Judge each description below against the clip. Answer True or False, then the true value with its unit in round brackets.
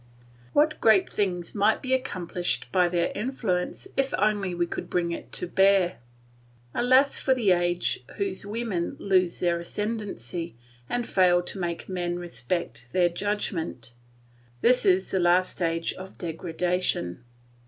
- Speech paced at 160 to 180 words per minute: False (140 wpm)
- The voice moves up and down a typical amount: True (3.1 semitones)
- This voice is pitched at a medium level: True (180 Hz)